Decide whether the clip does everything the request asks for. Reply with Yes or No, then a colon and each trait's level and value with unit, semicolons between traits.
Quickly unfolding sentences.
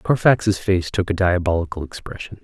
No: average, 150 wpm